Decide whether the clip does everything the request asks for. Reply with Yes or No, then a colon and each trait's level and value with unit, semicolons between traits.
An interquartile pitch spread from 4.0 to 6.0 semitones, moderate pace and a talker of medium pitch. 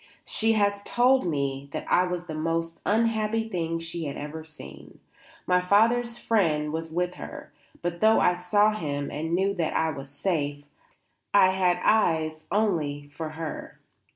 Yes: average, 4.5 semitones; average, 165 wpm; medium, 170 Hz